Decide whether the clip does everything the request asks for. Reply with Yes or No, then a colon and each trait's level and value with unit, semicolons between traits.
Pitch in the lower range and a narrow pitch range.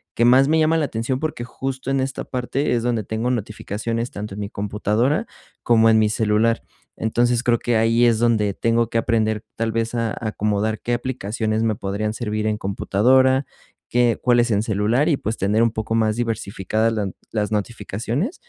Yes: low, 115 Hz; narrow, 2.2 semitones